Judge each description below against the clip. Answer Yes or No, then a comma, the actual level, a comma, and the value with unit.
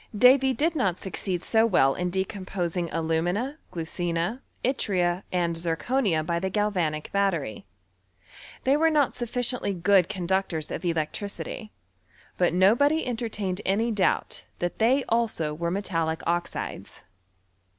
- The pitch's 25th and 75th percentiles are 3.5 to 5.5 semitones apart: Yes, average, 5.2 semitones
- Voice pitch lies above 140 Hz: Yes, high, 190 Hz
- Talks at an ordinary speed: No, slow, 130 wpm